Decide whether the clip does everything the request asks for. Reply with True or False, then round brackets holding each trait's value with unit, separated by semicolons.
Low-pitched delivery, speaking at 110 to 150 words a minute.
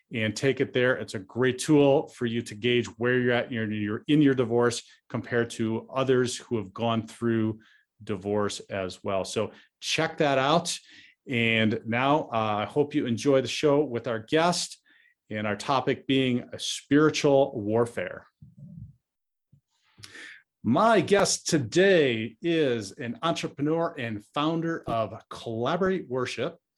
True (120 Hz; 140 wpm)